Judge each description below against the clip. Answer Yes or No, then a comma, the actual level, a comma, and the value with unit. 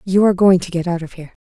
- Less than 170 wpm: No, fast, 335 wpm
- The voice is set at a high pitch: No, medium, 180 Hz